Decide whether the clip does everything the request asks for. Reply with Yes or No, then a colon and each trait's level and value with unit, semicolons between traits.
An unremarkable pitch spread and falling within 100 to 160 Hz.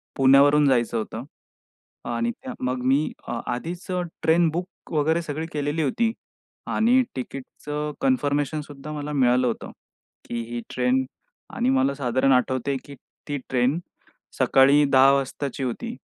Yes: average, 3.0 semitones; medium, 140 Hz